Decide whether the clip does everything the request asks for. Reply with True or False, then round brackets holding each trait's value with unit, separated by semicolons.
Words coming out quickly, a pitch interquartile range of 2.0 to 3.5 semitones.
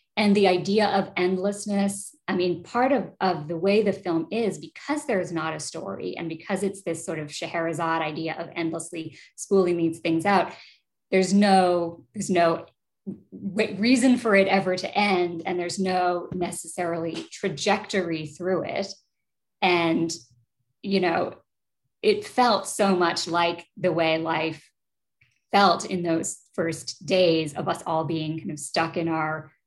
False (155 wpm; 3.0 semitones)